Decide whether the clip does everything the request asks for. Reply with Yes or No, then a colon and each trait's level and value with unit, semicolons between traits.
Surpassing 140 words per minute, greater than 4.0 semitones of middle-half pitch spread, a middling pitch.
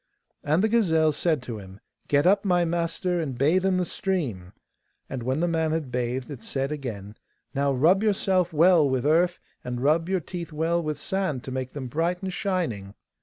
Yes: average, 195 wpm; average, 5.3 semitones; medium, 155 Hz